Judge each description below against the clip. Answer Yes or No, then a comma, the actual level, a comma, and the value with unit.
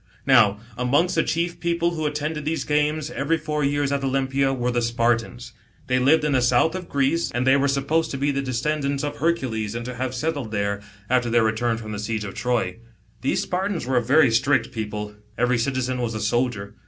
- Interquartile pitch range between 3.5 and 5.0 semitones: Yes, average, 4.1 semitones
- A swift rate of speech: Yes, fast, 210 wpm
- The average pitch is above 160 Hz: No, low, 130 Hz